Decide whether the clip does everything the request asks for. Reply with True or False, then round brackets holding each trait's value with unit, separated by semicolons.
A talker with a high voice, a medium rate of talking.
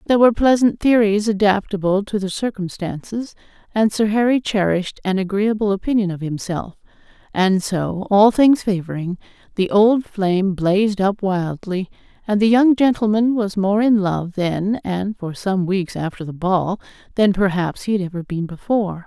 True (200 Hz; 160 wpm)